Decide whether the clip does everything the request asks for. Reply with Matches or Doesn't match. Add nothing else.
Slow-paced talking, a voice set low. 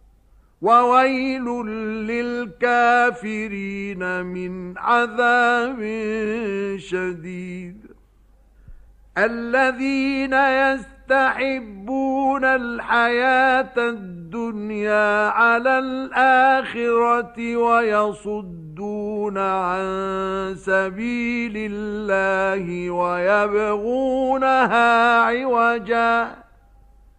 Doesn't match